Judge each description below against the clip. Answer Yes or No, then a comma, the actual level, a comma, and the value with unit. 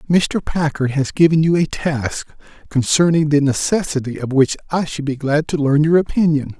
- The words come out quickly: No, average, 180 wpm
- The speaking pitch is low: No, medium, 150 Hz